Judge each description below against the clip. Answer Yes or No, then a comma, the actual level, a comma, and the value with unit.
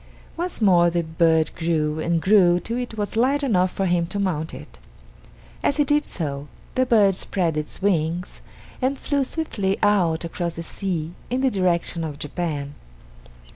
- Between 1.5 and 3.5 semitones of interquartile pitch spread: No, average, 4.8 semitones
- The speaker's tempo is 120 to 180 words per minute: Yes, average, 170 wpm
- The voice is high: No, medium, 180 Hz